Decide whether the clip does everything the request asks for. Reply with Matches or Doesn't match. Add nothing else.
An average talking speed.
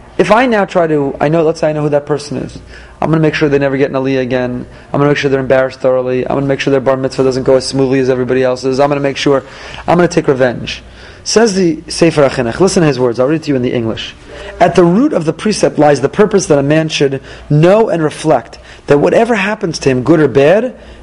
Doesn't match